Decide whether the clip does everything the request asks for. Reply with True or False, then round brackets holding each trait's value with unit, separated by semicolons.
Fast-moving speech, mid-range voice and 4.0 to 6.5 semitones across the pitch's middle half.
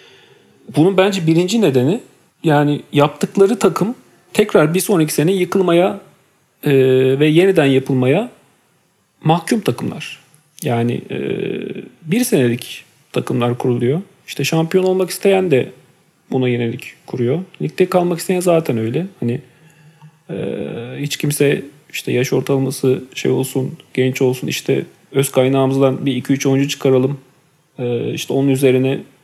False (125 wpm; 145 Hz; 5.0 semitones)